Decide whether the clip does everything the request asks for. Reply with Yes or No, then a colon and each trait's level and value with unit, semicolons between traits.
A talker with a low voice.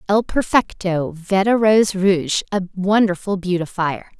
No: high, 190 Hz